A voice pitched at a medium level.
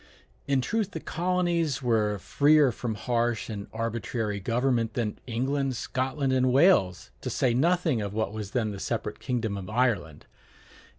No: low, 120 Hz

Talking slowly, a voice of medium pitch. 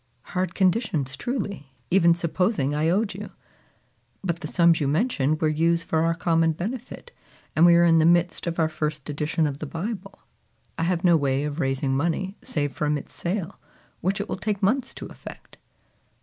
No: average, 185 wpm; medium, 165 Hz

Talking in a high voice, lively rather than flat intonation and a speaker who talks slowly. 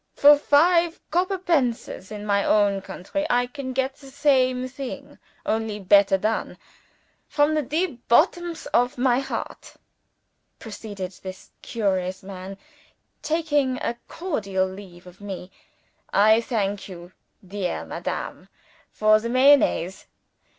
Yes: high, 235 Hz; wide, 6.3 semitones; slow, 120 wpm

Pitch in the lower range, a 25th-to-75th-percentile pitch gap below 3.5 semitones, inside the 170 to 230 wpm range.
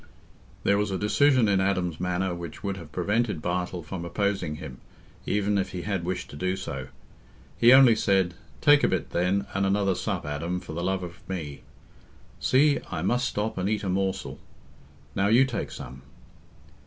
Yes: very low, 95 Hz; average, 2.9 semitones; average, 180 wpm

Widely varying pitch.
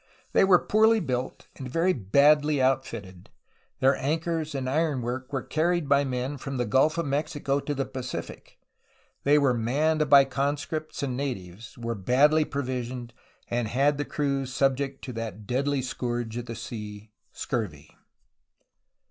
No: average, 3.3 semitones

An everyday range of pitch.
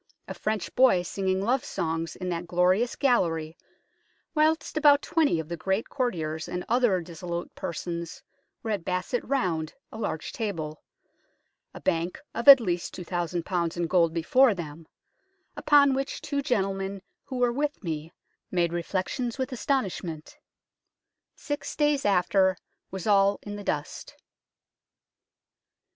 No: wide, 6.4 semitones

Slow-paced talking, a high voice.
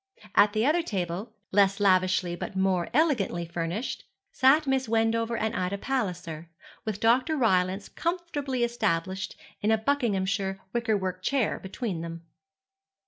Yes: slow, 130 wpm; high, 205 Hz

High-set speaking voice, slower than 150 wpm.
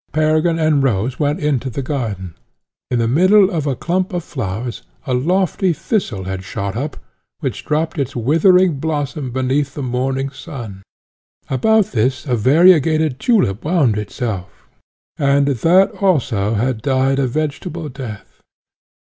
No: medium, 140 Hz; average, 140 wpm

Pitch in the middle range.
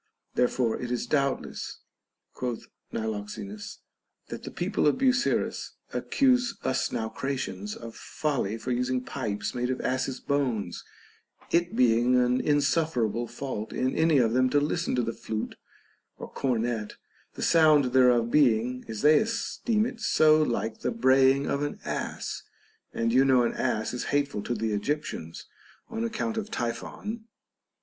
No: low, 130 Hz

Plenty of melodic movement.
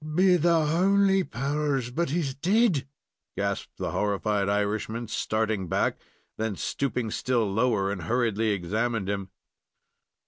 Yes: wide, 6.6 semitones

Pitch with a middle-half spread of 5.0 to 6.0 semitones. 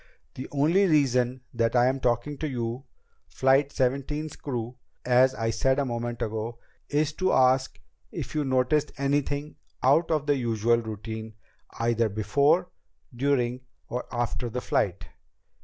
No: average, 3.3 semitones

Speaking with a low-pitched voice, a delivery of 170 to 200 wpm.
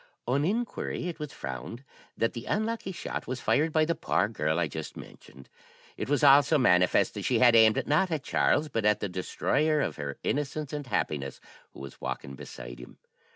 Yes: low, 125 Hz; average, 195 wpm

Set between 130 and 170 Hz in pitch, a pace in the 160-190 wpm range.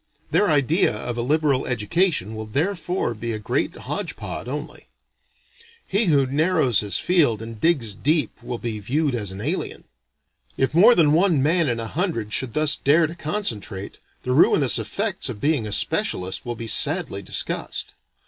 Yes: low, 135 Hz; average, 170 wpm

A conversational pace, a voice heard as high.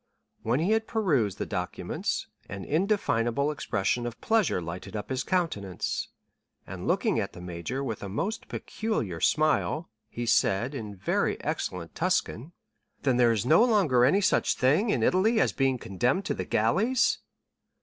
No: average, 160 wpm; low, 130 Hz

